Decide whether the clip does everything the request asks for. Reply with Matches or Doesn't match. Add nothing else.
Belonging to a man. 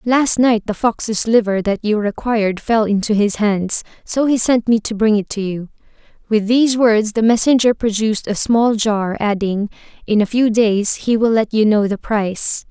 Doesn't match